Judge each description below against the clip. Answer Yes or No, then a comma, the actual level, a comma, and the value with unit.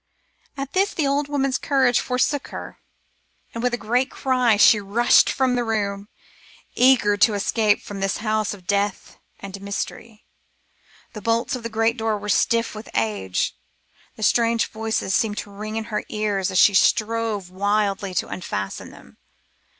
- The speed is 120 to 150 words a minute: No, average, 165 wpm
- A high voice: Yes, high, 215 Hz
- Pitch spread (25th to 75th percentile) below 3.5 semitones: Yes, average, 2.9 semitones